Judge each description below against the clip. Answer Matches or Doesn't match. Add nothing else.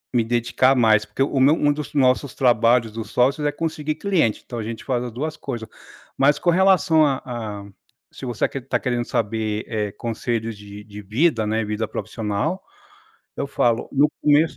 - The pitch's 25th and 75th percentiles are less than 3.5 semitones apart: Doesn't match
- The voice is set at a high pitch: Doesn't match